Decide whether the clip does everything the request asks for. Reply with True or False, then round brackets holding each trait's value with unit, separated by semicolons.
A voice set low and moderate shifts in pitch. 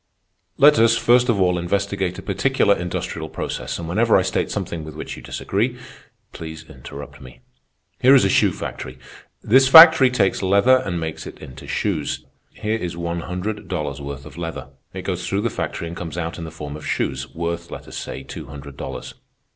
True (85 Hz; 5.0 semitones)